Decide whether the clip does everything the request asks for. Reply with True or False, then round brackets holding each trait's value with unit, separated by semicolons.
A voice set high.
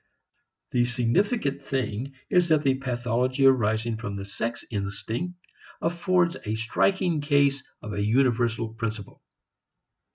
False (125 Hz)